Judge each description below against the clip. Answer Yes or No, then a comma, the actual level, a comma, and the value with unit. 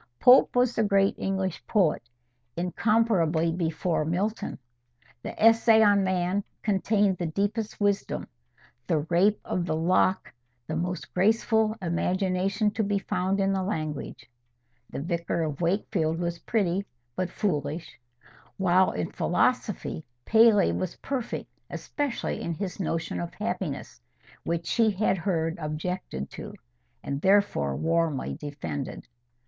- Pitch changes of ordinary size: Yes, average, 3.7 semitones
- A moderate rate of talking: No, slow, 125 wpm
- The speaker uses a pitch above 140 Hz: Yes, medium, 185 Hz